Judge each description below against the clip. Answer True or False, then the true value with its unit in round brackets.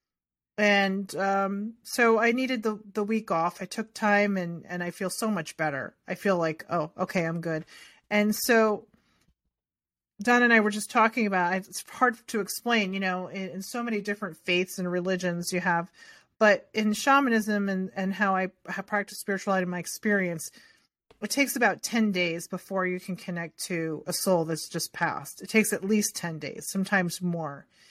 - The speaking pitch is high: True (195 Hz)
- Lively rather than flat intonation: False (3.1 semitones)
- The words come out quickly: False (190 wpm)